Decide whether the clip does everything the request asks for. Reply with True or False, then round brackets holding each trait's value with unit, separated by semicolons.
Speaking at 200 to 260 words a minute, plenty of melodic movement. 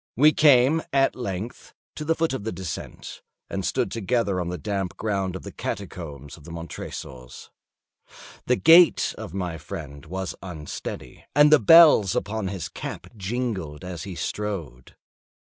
False (155 wpm; 6.5 semitones)